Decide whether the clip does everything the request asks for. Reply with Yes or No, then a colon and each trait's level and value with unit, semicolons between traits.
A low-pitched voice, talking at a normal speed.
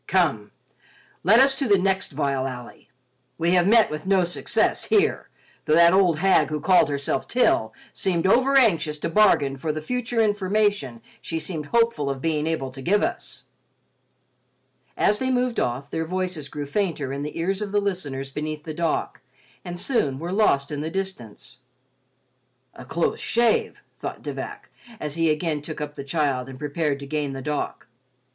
No: medium, 165 Hz; average, 175 wpm